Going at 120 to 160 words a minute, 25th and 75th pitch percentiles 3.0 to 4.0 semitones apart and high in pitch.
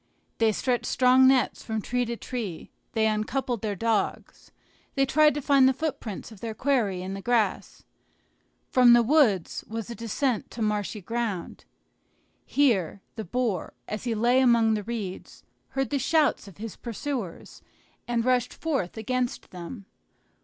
Yes: average, 155 wpm; average, 3.3 semitones; high, 235 Hz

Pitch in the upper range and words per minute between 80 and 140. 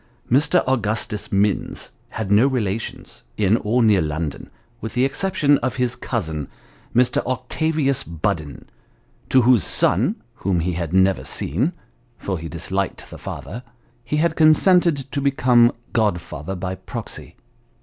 No: low, 115 Hz; slow, 135 wpm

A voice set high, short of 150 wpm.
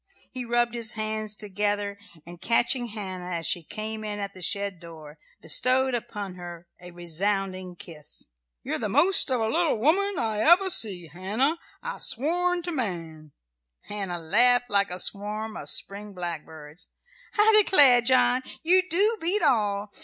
No: high, 210 Hz; average, 160 wpm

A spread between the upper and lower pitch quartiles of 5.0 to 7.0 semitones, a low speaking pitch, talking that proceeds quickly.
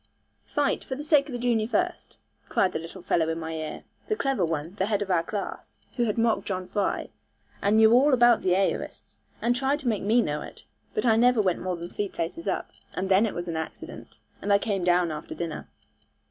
No: wide, 5.6 semitones; high, 205 Hz; fast, 230 wpm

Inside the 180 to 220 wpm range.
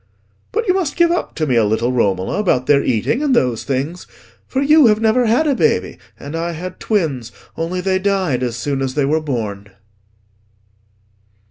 Yes: average, 190 wpm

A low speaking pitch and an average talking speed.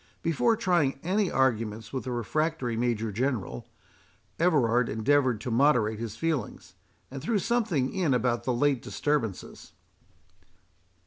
No: low, 130 Hz; slow, 125 wpm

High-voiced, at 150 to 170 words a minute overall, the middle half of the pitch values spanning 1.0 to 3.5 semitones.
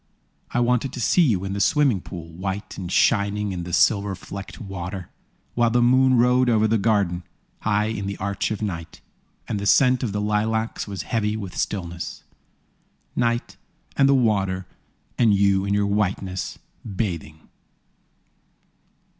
No: low, 105 Hz; average, 155 wpm; average, 3.1 semitones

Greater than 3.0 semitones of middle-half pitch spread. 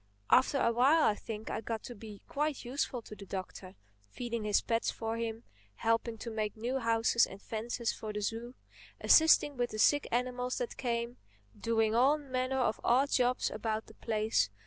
No: narrow, 2.4 semitones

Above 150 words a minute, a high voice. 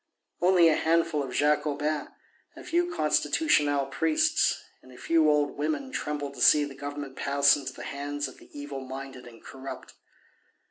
No: average, 165 wpm; medium, 145 Hz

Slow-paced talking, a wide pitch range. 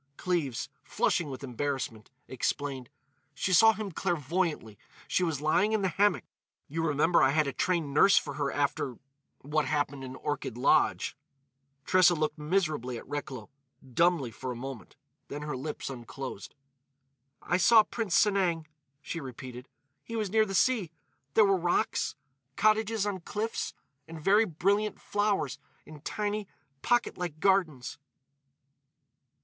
Yes: slow, 130 wpm; wide, 6.1 semitones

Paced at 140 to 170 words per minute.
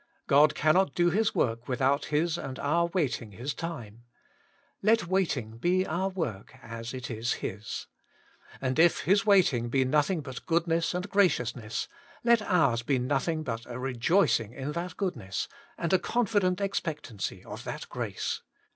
Yes: average, 165 wpm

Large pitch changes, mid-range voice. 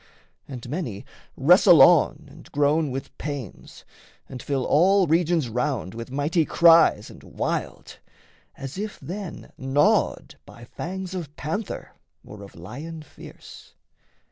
No: average, 5.0 semitones; medium, 145 Hz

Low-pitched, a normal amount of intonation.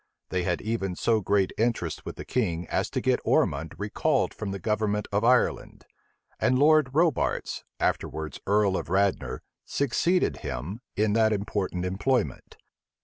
Yes: low, 105 Hz; average, 3.9 semitones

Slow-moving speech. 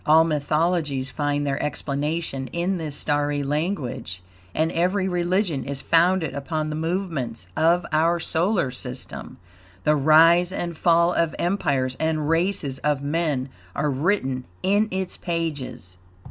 Yes: slow, 130 wpm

